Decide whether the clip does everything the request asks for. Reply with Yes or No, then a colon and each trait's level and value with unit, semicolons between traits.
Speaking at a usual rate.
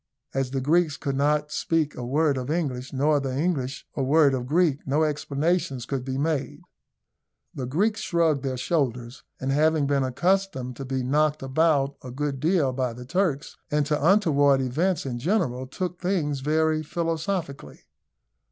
Yes: average, 165 wpm